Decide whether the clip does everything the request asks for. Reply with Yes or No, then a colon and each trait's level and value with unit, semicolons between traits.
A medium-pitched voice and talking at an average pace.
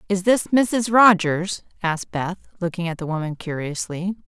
Yes: medium, 180 Hz; average, 155 wpm